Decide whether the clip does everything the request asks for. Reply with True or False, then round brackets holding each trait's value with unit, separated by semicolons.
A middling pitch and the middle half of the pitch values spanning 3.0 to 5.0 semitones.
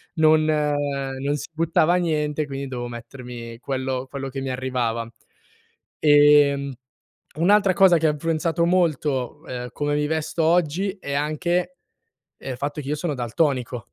True (145 Hz; 3.3 semitones)